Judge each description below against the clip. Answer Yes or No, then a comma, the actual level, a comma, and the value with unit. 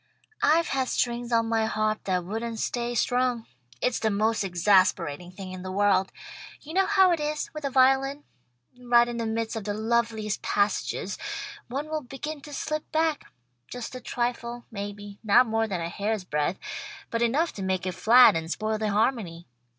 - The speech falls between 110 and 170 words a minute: No, average, 180 wpm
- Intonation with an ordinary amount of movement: Yes, average, 4.0 semitones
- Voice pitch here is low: No, high, 225 Hz